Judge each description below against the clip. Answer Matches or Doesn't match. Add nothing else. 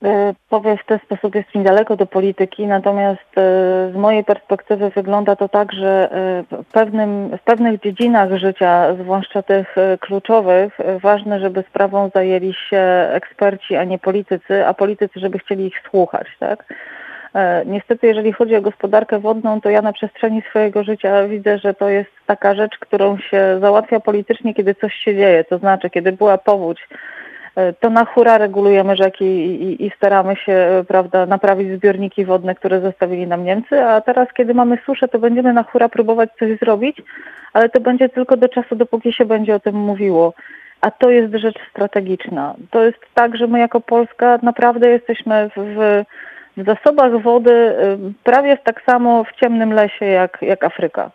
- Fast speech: Matches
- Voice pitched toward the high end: Matches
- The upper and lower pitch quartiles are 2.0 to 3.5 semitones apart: Matches